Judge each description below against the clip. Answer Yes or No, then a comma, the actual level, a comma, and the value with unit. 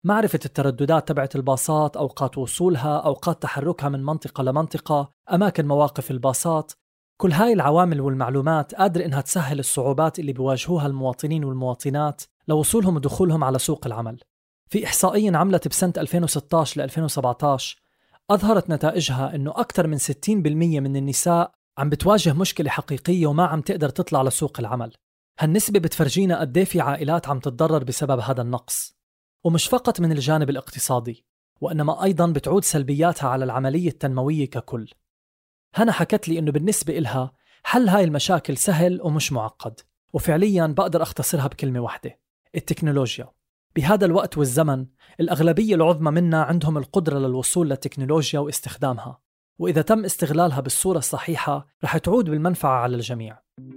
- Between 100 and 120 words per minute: No, fast, 135 wpm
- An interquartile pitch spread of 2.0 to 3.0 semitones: No, average, 4.1 semitones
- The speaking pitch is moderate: Yes, medium, 155 Hz